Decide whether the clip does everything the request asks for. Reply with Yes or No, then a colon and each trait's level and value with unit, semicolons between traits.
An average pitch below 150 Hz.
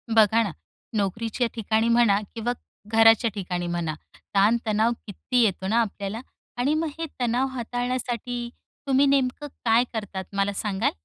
No: high, 225 Hz